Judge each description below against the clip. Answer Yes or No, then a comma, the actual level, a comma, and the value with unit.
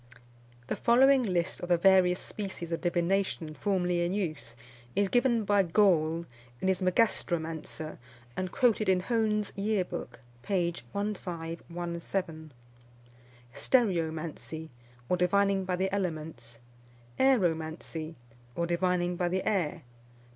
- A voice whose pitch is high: No, medium, 180 Hz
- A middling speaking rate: No, slow, 115 wpm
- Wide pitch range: No, average, 3.2 semitones